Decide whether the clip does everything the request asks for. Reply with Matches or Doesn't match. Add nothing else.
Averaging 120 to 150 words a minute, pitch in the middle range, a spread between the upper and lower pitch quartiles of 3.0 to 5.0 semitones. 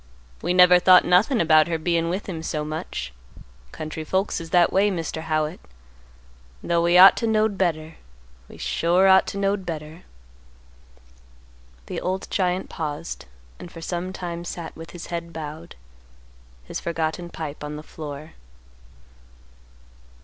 Doesn't match